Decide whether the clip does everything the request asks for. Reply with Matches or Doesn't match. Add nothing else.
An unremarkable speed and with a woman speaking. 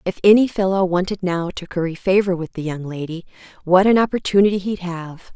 Matches